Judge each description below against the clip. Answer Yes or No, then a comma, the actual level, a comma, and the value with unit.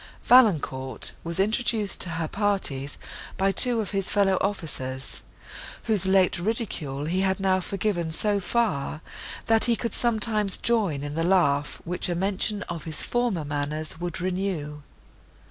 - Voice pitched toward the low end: No, high, 190 Hz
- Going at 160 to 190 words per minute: No, average, 145 wpm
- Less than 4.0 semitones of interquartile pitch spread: No, average, 4.8 semitones